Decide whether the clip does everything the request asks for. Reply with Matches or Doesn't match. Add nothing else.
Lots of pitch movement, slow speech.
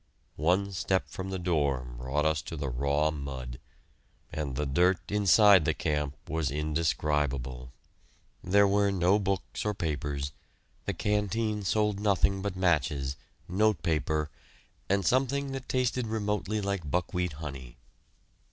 Matches